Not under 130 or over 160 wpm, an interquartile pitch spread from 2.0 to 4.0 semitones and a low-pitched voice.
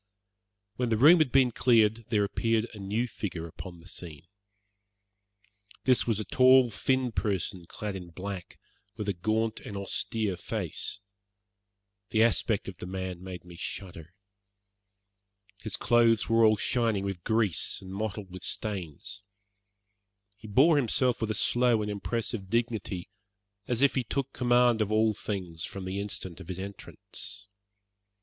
Yes: average, 150 wpm; average, 3.7 semitones; low, 105 Hz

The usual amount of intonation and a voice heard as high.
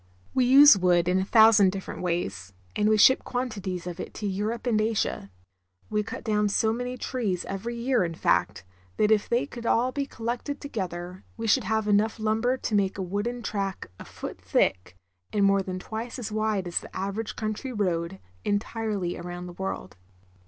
Yes: average, 3.7 semitones; high, 210 Hz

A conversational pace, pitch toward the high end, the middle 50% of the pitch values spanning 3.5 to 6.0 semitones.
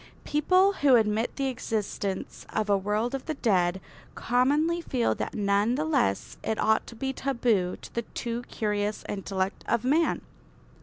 Yes: average, 160 wpm; high, 230 Hz; average, 4.8 semitones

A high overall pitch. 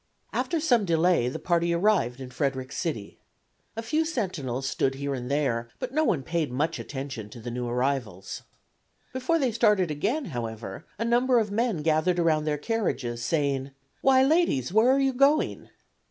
No: medium, 160 Hz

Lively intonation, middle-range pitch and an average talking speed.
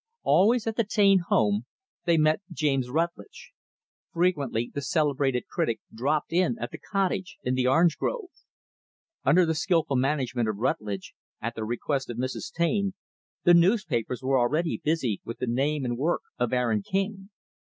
Yes: wide, 6.1 semitones; medium, 145 Hz; average, 160 wpm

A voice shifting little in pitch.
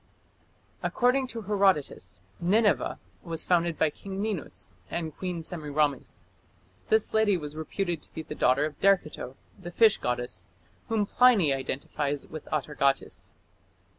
No: wide, 5.4 semitones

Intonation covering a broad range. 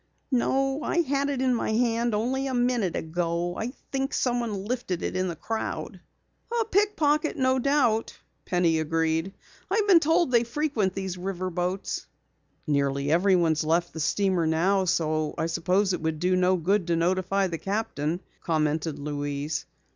Yes: wide, 6.9 semitones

